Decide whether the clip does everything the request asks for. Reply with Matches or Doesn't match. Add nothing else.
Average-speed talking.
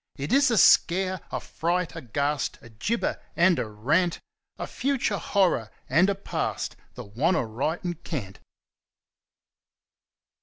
Doesn't match